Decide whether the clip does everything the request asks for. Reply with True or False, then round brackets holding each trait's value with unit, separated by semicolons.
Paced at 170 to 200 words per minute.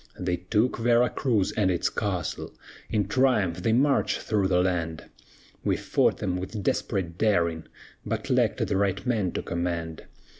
False (155 wpm)